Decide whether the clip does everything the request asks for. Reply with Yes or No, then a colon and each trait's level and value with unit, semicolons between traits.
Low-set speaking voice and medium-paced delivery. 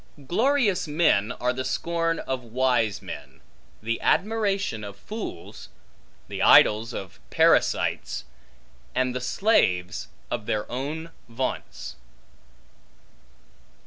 No: low, 130 Hz; slow, 100 wpm